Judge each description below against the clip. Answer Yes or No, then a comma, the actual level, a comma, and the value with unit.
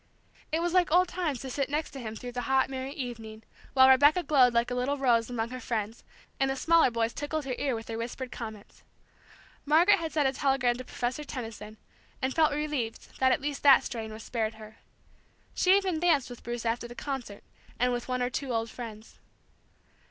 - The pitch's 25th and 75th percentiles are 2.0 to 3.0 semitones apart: No, average, 3.8 semitones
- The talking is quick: Yes, fast, 210 wpm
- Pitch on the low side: No, very high, 255 Hz